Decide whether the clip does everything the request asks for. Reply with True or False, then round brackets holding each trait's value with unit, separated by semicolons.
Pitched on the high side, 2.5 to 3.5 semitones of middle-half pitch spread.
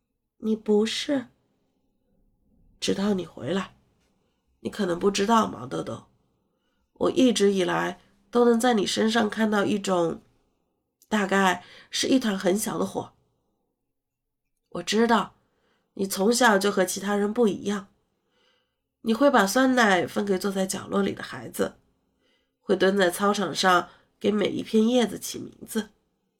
True (205 Hz; 3.0 semitones)